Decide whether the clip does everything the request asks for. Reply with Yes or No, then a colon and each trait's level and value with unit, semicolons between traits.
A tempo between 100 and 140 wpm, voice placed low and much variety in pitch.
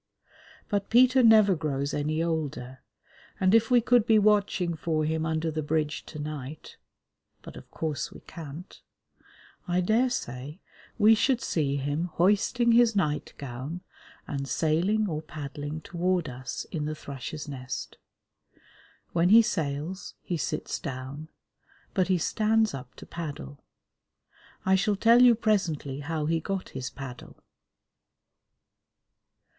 No: slow, 135 wpm; medium, 160 Hz; wide, 5.8 semitones